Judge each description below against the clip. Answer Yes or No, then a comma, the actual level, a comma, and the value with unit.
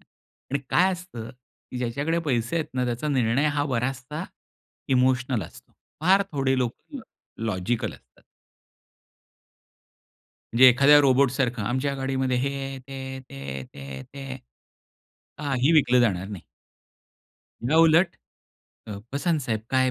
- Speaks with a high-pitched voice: No, low, 130 Hz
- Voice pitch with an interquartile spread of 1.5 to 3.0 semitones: Yes, average, 2.7 semitones